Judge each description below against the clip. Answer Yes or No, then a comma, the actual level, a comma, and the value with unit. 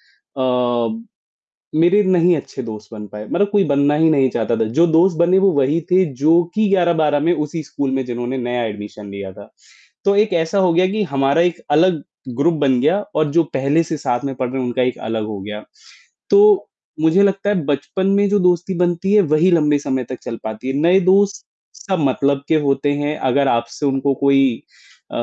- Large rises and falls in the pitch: Yes, wide, 5.9 semitones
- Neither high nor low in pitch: Yes, medium, 145 Hz